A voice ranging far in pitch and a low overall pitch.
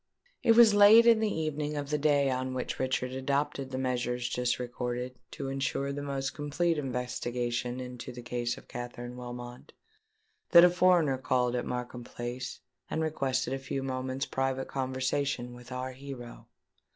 No: narrow, 2.5 semitones; low, 130 Hz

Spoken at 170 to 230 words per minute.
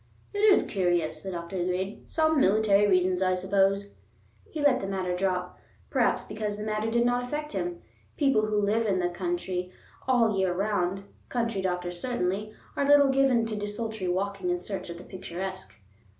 Yes: average, 180 wpm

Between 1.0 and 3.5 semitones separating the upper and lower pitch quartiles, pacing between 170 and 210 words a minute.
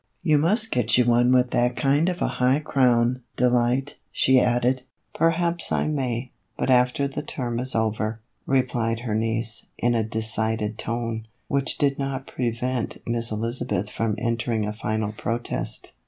No: average, 2.7 semitones; average, 155 wpm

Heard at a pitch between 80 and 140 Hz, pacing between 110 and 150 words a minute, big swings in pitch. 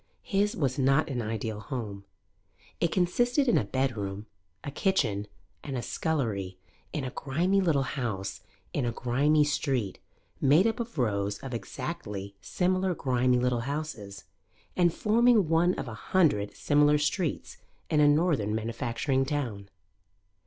Yes: low, 135 Hz; average, 140 wpm; wide, 6.4 semitones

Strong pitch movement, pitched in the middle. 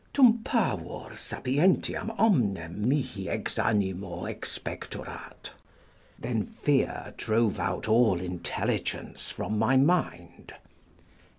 No: wide, 7.6 semitones; low, 110 Hz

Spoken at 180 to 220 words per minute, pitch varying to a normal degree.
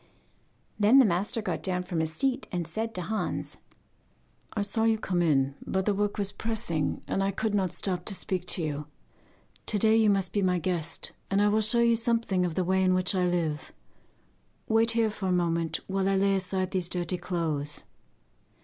Yes: fast, 205 wpm; average, 3.3 semitones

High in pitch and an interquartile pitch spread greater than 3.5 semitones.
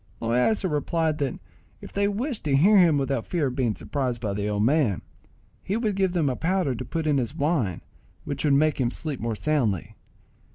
No: medium, 145 Hz; wide, 5.5 semitones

